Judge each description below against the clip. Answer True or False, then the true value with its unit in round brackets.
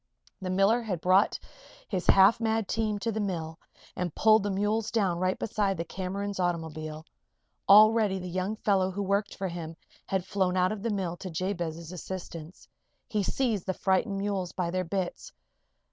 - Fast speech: False (175 wpm)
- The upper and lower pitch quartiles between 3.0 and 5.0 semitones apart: False (2.5 semitones)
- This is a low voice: False (190 Hz)